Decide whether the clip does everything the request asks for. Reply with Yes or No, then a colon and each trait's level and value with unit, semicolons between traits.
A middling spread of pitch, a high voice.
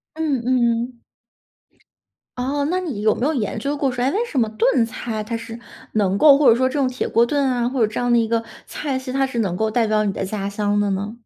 Yes: average, 3.7 semitones; high, 240 Hz